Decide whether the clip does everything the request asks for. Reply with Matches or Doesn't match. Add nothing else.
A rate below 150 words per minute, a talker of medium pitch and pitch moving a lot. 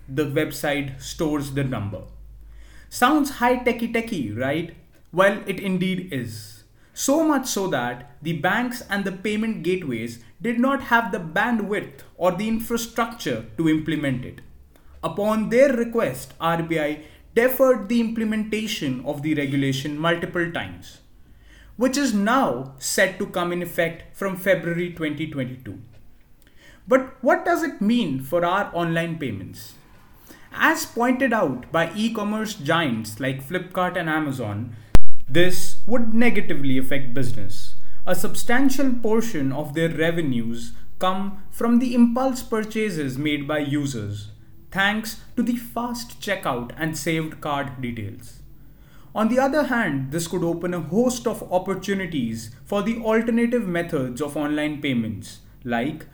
Matches